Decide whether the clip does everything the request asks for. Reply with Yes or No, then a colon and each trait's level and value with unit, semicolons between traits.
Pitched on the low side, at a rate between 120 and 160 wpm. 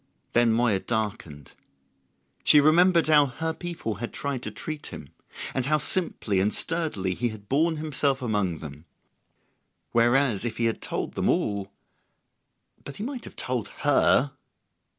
Yes: low, 125 Hz; average, 150 wpm